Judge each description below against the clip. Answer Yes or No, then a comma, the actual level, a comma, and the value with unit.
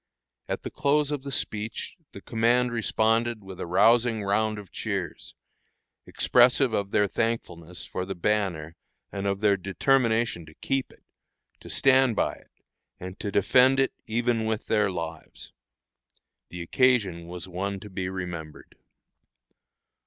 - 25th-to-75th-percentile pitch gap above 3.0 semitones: Yes, average, 4.3 semitones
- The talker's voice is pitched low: Yes, low, 105 Hz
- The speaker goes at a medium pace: Yes, average, 145 wpm